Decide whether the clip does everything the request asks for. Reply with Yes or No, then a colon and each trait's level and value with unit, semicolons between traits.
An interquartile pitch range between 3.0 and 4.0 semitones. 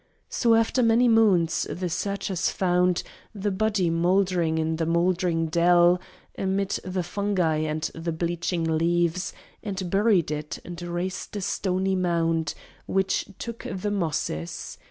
No: narrow, 2.6 semitones